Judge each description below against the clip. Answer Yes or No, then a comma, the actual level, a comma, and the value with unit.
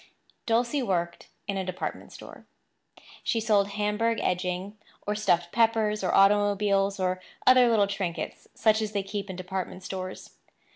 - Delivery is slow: No, average, 145 wpm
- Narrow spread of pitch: Yes, narrow, 2.3 semitones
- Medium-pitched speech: No, high, 200 Hz